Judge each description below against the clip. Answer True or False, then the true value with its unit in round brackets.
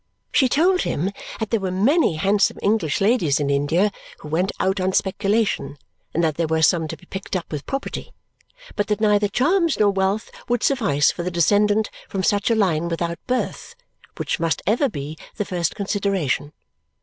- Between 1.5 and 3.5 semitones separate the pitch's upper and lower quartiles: False (4.5 semitones)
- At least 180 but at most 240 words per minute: True (185 wpm)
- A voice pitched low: False (195 Hz)